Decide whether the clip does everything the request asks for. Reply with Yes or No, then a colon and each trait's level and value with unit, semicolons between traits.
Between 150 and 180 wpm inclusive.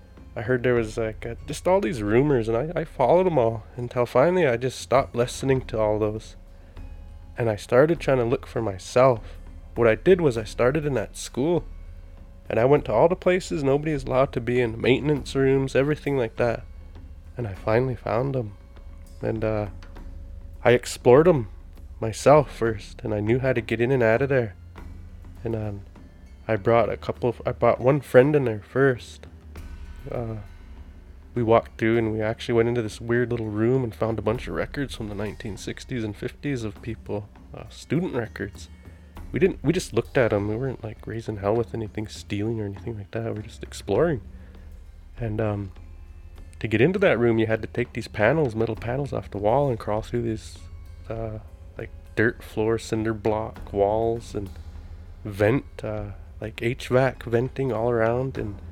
No: average, 190 wpm